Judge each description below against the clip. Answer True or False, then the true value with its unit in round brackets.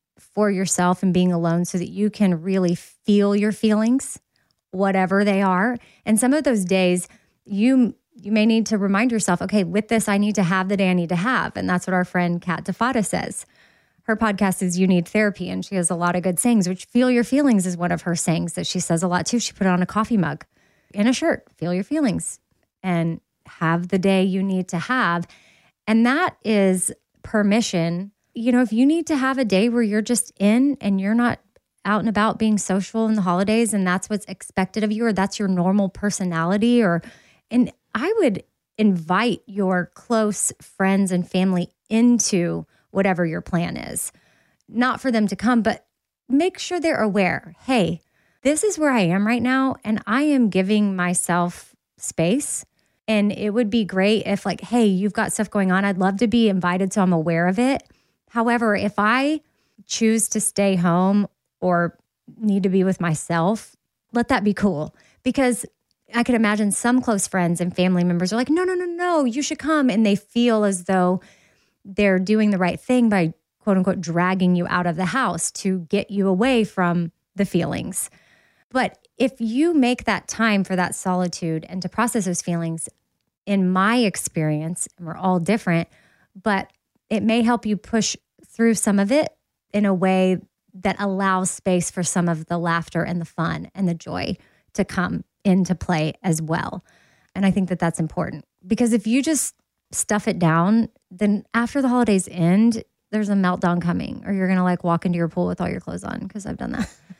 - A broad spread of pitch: False (4.0 semitones)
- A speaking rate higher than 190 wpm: True (200 wpm)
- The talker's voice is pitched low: False (200 Hz)